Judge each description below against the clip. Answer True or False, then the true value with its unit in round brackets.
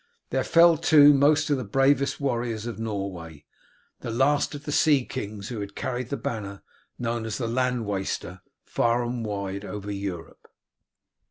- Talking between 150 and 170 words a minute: True (165 wpm)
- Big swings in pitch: False (5.0 semitones)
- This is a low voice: True (115 Hz)